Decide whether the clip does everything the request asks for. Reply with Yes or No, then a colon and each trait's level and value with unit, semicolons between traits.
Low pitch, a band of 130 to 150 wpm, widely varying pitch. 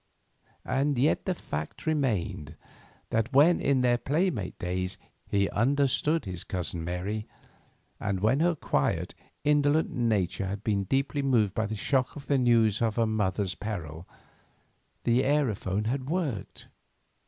Yes: low, 115 Hz; average, 140 wpm; wide, 6.1 semitones